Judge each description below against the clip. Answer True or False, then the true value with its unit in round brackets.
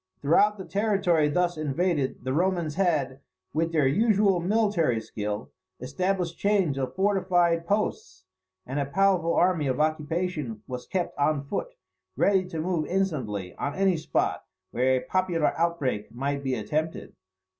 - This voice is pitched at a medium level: True (165 Hz)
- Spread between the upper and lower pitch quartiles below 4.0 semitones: False (5.2 semitones)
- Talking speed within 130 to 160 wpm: True (145 wpm)